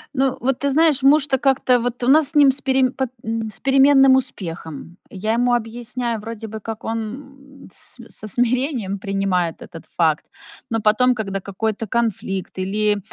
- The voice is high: Yes, high, 230 Hz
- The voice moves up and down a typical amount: Yes, average, 4.2 semitones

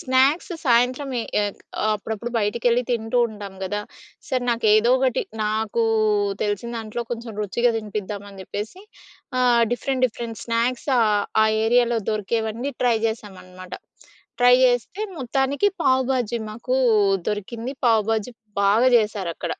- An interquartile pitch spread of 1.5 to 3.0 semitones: Yes, average, 2.7 semitones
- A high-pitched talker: Yes, high, 230 Hz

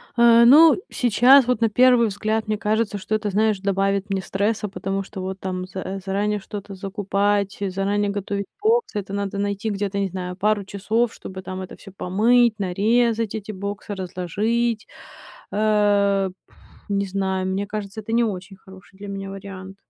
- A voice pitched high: Yes, high, 200 Hz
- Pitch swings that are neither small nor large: No, narrow, 1.9 semitones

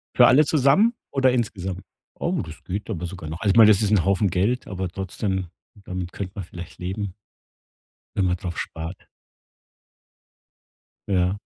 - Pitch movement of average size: Yes, average, 3.3 semitones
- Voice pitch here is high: No, very low, 95 Hz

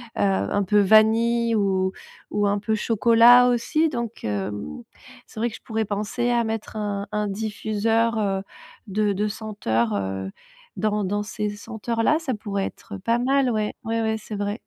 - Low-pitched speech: No, high, 215 Hz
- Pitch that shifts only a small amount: Yes, narrow, 2.2 semitones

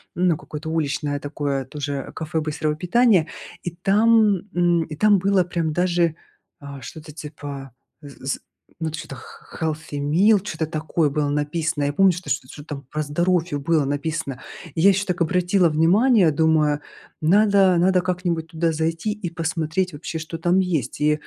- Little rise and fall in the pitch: No, average, 3.3 semitones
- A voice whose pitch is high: No, medium, 160 Hz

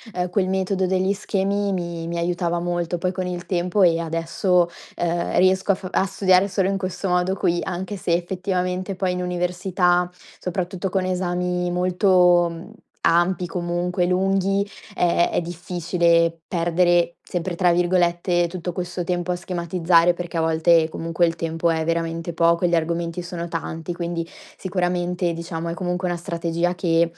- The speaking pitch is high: No, medium, 175 Hz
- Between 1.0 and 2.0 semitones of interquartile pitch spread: Yes, narrow, 1.4 semitones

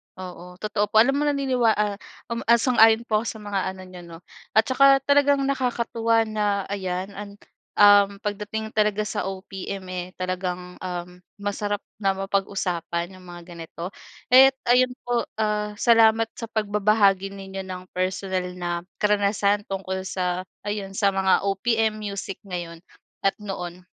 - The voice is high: Yes, high, 200 Hz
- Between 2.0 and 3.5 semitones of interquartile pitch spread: Yes, average, 2.9 semitones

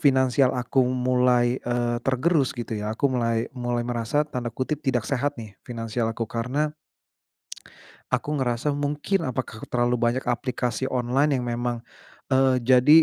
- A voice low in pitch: Yes, low, 125 Hz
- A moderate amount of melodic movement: No, narrow, 2.0 semitones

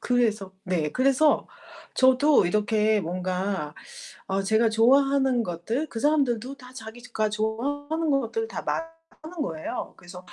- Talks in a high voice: Yes, high, 235 Hz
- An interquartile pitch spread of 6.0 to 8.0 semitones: No, wide, 5.6 semitones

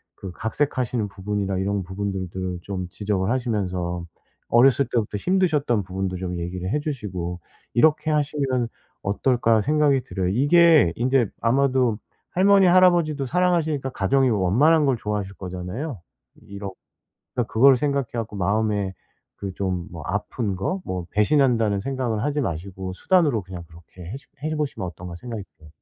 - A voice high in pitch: No, low, 110 Hz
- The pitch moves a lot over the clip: Yes, wide, 6.7 semitones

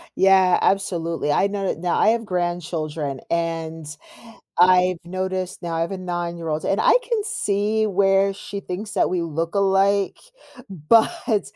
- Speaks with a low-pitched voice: No, medium, 185 Hz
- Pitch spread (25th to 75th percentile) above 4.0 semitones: No, average, 2.9 semitones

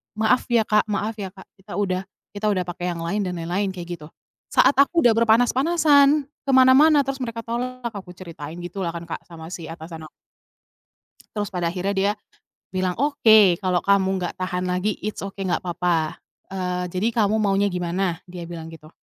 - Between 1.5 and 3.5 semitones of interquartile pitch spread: No, average, 3.9 semitones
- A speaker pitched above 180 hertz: Yes, high, 190 Hz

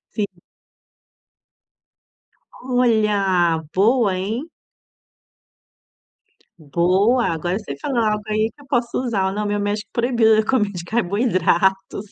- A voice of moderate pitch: No, high, 210 Hz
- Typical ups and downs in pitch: Yes, average, 3.6 semitones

